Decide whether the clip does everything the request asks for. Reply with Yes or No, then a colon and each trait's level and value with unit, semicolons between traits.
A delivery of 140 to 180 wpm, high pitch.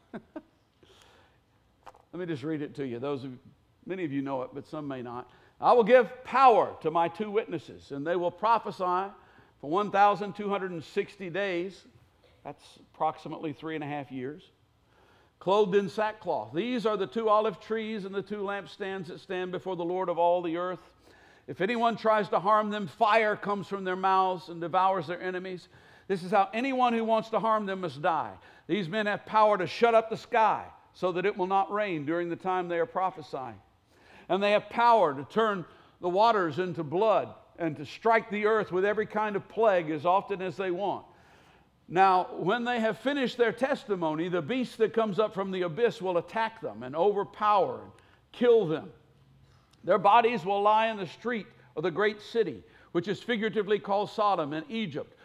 No: average, 190 wpm; high, 195 Hz